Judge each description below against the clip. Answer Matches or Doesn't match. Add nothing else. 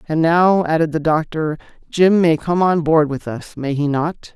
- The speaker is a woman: Doesn't match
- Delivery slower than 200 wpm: Doesn't match